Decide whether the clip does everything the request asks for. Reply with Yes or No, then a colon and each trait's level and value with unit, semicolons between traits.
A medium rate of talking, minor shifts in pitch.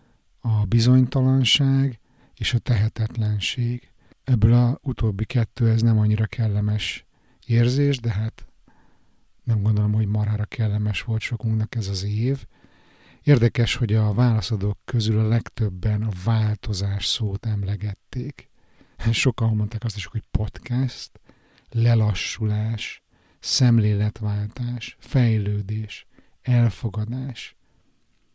No: slow, 100 wpm; narrow, 2.3 semitones